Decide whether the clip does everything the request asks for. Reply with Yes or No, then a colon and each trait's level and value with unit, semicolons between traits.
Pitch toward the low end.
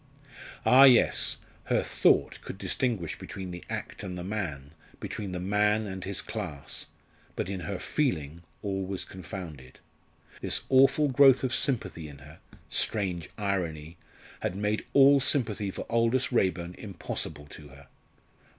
Yes: very low, 95 Hz